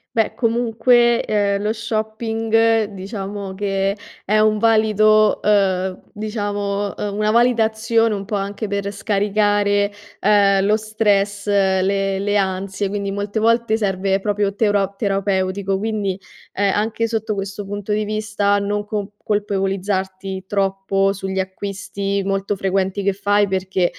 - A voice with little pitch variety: Yes, narrow, 1.5 semitones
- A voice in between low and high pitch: No, high, 205 Hz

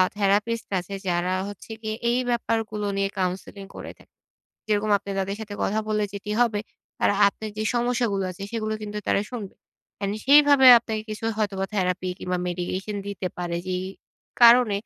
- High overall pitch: Yes, high, 205 Hz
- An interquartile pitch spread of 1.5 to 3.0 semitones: Yes, narrow, 2.4 semitones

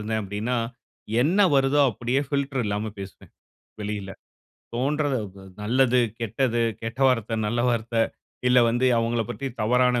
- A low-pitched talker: Yes, low, 120 Hz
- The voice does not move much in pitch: No, average, 3.2 semitones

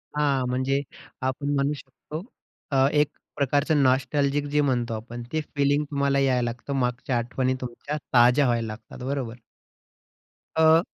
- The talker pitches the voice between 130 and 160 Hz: Yes, low, 135 Hz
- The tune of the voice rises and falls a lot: No, average, 2.7 semitones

